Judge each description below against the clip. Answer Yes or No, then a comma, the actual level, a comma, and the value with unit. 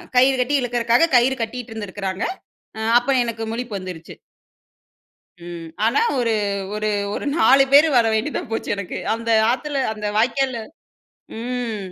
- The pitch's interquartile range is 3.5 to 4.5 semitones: No, average, 2.9 semitones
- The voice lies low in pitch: No, high, 235 Hz